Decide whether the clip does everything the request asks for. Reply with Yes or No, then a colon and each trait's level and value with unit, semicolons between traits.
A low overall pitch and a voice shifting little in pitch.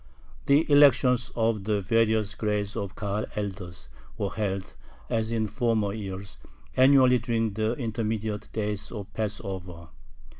Yes: low, 110 Hz; narrow, 2.3 semitones